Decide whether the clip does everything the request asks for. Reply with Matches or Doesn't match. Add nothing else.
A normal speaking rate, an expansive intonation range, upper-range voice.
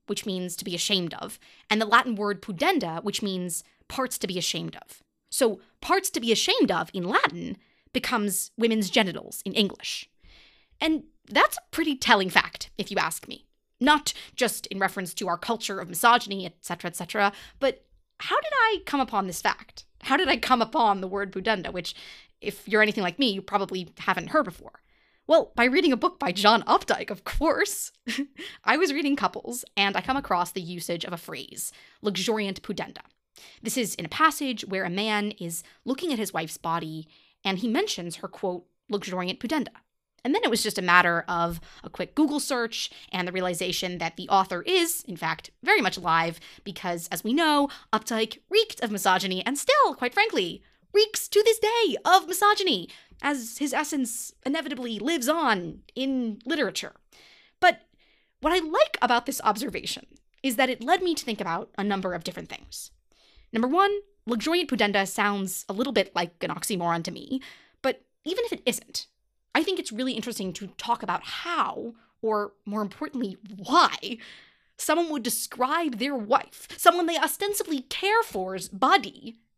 Matches